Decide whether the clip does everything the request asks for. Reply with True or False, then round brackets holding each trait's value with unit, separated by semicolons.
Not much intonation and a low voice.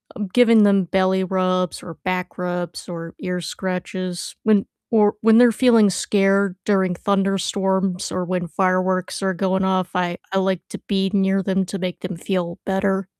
False (1.3 semitones; 190 Hz)